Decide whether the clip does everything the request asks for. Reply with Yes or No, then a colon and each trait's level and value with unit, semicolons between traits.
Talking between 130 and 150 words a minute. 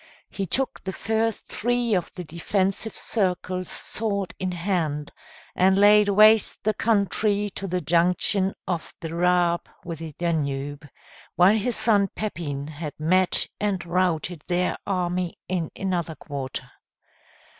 Yes: slow, 135 wpm